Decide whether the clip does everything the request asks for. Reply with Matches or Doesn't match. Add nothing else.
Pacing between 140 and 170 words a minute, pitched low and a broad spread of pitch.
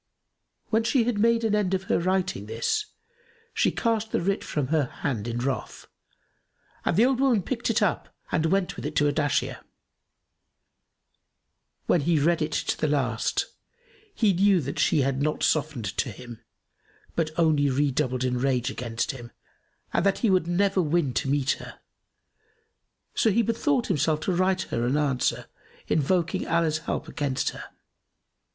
Doesn't match